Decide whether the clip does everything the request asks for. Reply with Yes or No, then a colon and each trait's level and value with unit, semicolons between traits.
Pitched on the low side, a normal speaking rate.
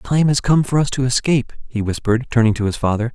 No: low, 125 Hz; fast, 265 wpm